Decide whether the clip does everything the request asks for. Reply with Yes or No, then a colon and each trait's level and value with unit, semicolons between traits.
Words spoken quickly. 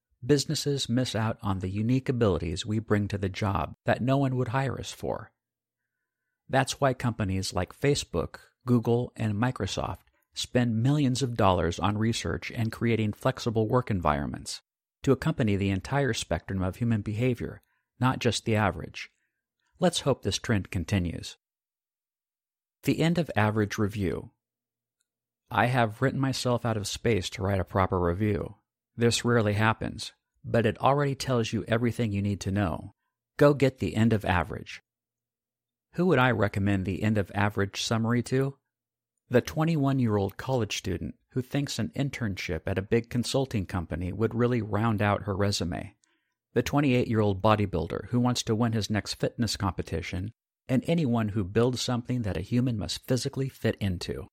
No: average, 160 wpm